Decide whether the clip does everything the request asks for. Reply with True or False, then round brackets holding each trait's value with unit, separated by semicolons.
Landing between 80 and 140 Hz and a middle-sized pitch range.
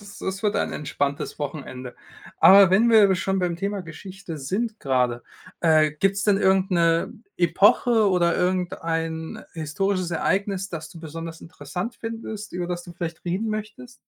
False (180 Hz; 3.6 semitones)